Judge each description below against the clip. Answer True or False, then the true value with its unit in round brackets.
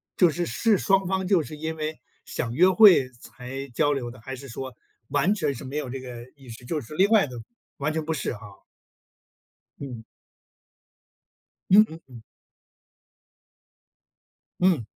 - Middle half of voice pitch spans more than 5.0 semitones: True (5.5 semitones)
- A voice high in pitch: False (145 Hz)